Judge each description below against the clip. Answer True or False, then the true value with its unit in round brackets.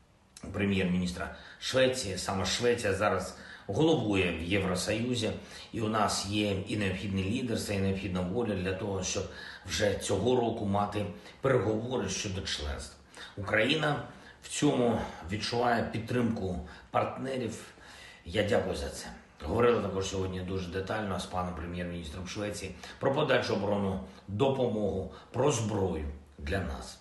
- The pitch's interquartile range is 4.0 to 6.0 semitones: False (3.0 semitones)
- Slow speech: False (120 wpm)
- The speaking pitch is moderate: False (100 Hz)